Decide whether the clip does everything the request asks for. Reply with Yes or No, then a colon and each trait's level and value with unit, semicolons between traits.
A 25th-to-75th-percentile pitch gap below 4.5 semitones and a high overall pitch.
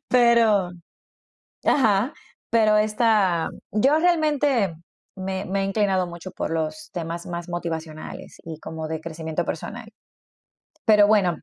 No: average, 4.8 semitones; high, 195 Hz